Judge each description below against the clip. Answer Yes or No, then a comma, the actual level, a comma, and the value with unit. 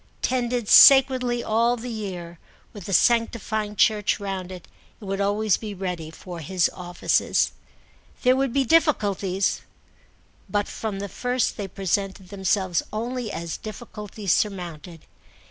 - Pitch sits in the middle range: No, high, 205 Hz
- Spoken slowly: Yes, slow, 130 wpm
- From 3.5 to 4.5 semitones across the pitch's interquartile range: Yes, average, 3.8 semitones